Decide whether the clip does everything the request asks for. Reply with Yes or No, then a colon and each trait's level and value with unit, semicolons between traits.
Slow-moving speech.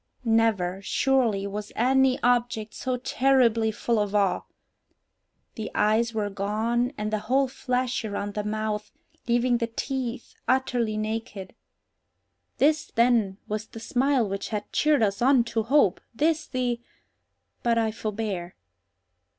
Yes: slow, 130 wpm